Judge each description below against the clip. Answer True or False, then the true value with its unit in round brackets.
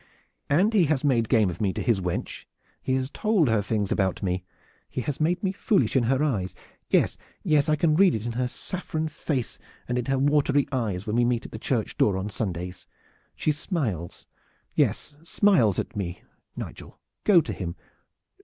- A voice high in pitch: False (125 Hz)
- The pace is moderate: True (190 wpm)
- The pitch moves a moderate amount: False (6.9 semitones)